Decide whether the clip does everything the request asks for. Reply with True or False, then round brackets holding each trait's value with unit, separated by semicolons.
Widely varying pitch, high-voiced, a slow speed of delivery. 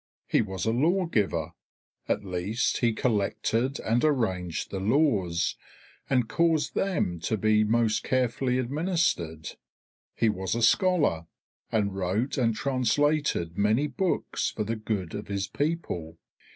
False (6.1 semitones; 110 Hz; 130 wpm)